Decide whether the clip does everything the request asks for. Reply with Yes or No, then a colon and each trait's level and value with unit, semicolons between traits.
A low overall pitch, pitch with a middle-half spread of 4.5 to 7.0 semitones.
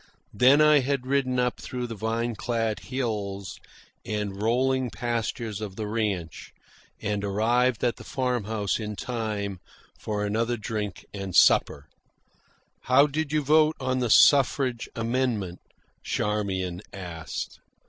No: low, 115 Hz; average, 3.6 semitones